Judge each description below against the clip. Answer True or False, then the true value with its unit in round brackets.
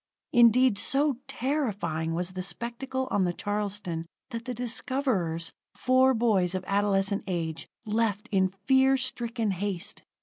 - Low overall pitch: False (210 Hz)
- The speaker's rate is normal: False (130 wpm)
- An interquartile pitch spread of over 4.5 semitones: True (5.3 semitones)